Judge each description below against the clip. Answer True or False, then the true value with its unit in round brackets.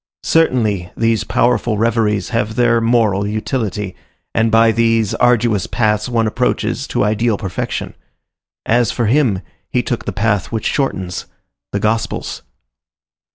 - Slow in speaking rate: True (125 wpm)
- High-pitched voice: False (110 Hz)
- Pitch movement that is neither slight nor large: False (2.1 semitones)